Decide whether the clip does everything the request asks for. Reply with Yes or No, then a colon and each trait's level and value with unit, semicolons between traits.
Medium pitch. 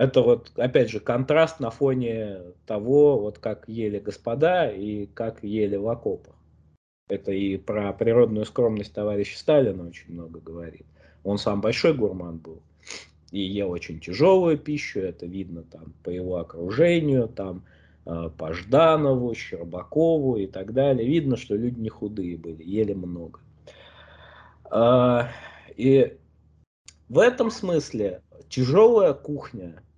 No: low, 105 Hz